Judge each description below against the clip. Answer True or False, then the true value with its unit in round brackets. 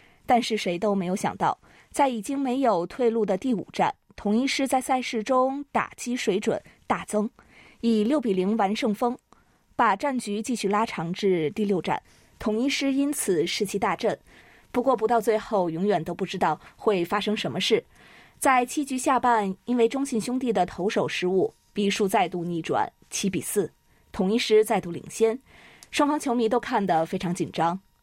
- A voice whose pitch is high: True (220 Hz)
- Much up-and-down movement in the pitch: False (4.4 semitones)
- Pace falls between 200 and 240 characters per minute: False (255 characters per minute)